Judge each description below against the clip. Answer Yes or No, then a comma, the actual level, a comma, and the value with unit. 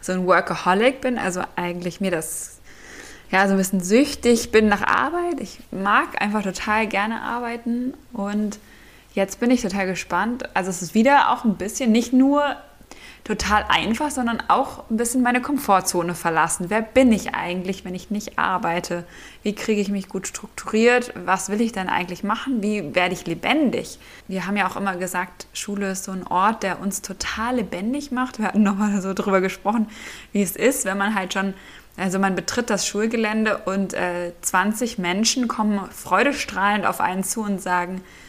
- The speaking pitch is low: No, high, 205 Hz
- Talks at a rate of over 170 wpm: Yes, average, 180 wpm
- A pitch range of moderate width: Yes, average, 3.7 semitones